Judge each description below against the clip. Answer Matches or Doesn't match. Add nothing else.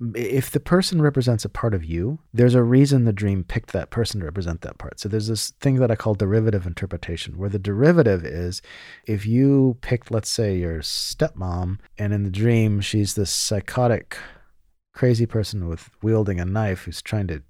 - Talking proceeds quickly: Doesn't match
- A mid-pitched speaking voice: Doesn't match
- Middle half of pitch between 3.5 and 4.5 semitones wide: Matches